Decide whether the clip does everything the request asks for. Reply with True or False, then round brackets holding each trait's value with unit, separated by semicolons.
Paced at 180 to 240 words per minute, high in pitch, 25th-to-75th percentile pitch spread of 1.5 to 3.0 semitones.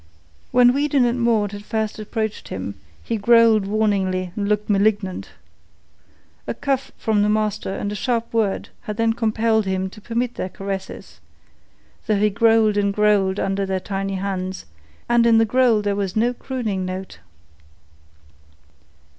False (155 wpm; 210 Hz; 2.6 semitones)